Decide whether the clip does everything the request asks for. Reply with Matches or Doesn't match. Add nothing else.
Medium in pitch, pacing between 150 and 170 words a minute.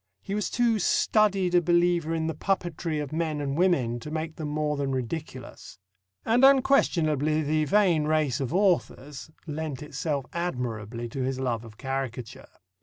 Matches